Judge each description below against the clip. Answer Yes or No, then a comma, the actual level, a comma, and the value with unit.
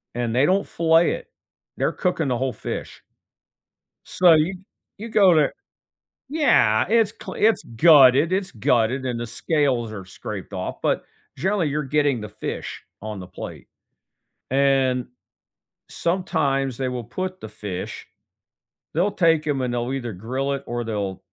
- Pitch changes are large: Yes, wide, 6.1 semitones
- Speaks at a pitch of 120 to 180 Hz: Yes, low, 135 Hz